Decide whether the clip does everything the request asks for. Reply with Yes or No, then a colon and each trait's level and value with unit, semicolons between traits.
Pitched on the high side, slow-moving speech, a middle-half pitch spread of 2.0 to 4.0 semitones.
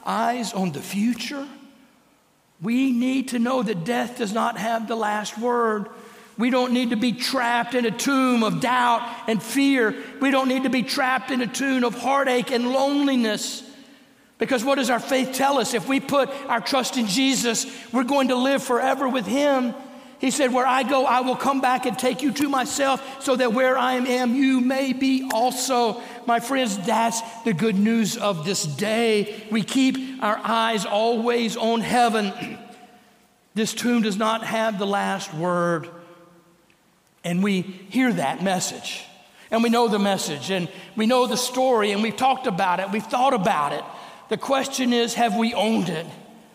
No: high, 240 Hz; average, 180 wpm; average, 2.8 semitones